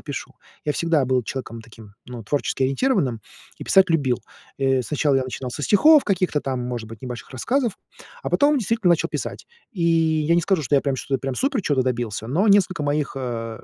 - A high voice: No, medium, 140 Hz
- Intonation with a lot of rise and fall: Yes, wide, 6.0 semitones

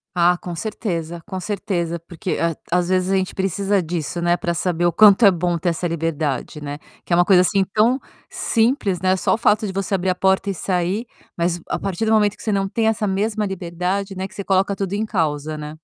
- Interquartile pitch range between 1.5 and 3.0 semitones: Yes, average, 2.7 semitones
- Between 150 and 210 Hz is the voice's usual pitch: Yes, medium, 185 Hz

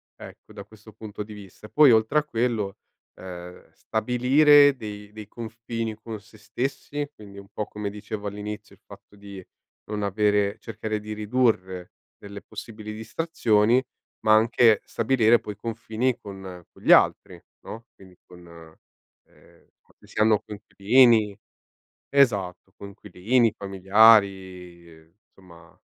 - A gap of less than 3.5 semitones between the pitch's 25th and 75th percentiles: Yes, narrow, 2.4 semitones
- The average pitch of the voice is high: No, low, 105 Hz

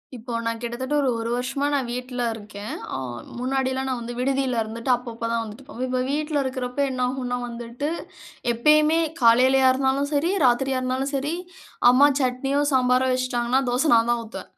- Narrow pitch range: Yes, narrow, 2.1 semitones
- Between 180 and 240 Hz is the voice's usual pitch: No, very high, 255 Hz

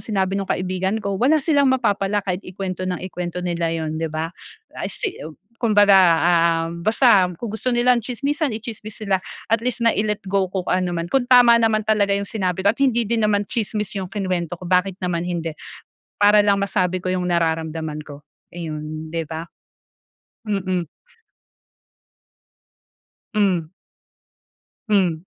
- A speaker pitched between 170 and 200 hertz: Yes, high, 190 Hz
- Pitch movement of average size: Yes, average, 3.9 semitones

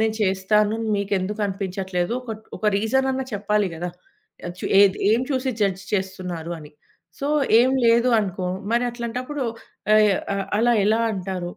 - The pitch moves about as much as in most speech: Yes, average, 3.6 semitones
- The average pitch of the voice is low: No, high, 210 Hz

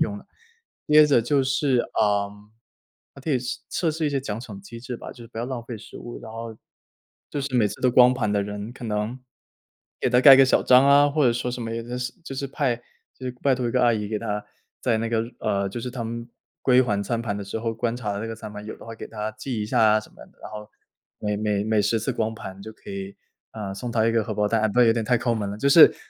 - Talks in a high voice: No, low, 115 Hz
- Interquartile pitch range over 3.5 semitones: No, average, 3.0 semitones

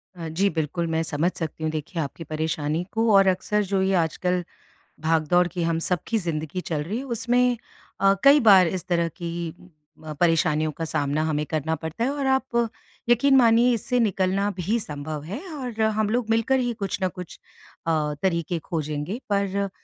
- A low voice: No, medium, 180 Hz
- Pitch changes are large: Yes, wide, 5.7 semitones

